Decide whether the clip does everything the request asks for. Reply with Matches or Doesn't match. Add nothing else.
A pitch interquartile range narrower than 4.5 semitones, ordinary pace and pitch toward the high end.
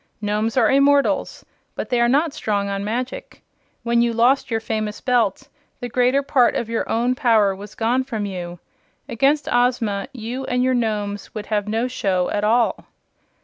Matches